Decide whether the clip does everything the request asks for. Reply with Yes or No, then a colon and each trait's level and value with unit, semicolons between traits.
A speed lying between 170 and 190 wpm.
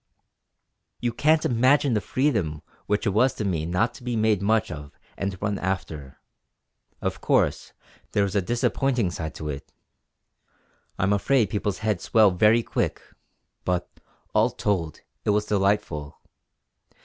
No: average, 145 wpm